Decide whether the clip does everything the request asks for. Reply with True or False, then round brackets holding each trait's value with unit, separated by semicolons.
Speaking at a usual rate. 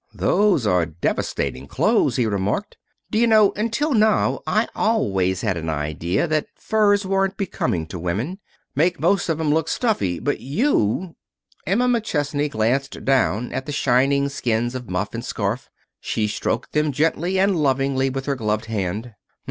True (160 wpm)